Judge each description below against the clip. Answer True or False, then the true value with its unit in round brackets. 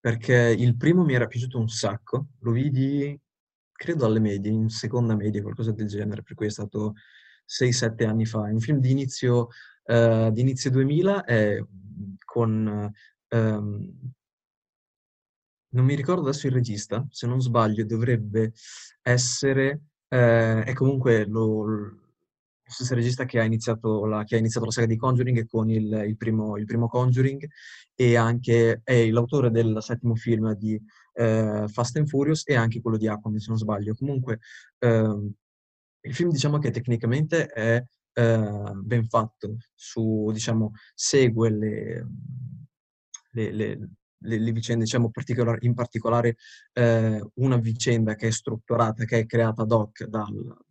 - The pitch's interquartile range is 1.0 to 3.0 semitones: True (2.4 semitones)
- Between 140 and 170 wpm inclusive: True (150 wpm)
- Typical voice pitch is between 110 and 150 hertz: True (115 Hz)